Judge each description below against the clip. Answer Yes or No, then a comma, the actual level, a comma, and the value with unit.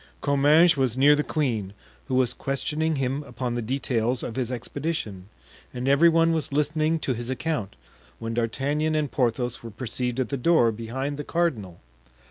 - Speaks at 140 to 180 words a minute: Yes, average, 170 wpm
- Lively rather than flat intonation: No, average, 4.1 semitones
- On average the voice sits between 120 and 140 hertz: Yes, low, 135 Hz